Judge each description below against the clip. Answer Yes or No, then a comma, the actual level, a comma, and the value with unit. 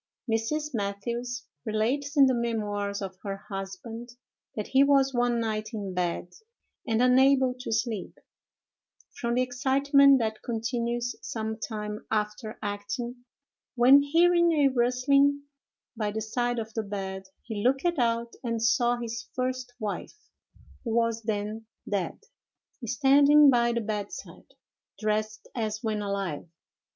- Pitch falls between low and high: No, high, 235 Hz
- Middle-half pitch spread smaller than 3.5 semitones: Yes, average, 3.1 semitones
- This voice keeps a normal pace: No, slow, 130 wpm